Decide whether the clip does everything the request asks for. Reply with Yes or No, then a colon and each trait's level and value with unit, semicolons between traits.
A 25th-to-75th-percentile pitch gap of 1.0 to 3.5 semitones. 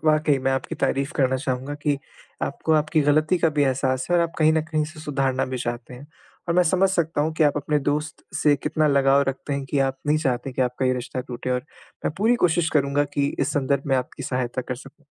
Yes: average, 2.8 semitones